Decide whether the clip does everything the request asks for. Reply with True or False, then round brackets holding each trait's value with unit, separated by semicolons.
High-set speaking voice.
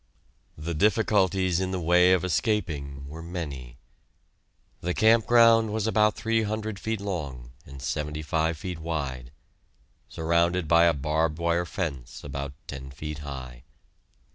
False (85 Hz)